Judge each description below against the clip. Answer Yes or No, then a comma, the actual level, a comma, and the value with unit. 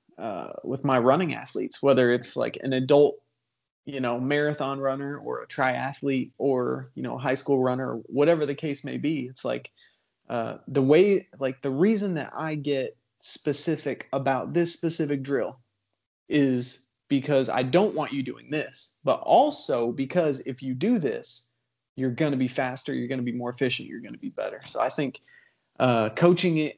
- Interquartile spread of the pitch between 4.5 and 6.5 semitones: No, narrow, 2.6 semitones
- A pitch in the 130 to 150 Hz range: Yes, low, 135 Hz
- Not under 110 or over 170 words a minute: No, average, 180 wpm